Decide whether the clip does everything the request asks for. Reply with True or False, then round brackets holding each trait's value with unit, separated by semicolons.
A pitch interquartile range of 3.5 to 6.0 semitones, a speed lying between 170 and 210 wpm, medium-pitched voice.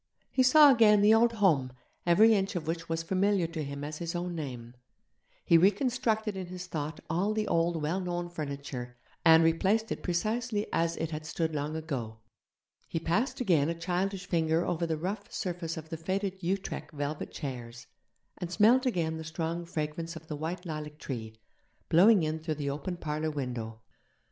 True (3.9 semitones; 180 wpm; 165 Hz)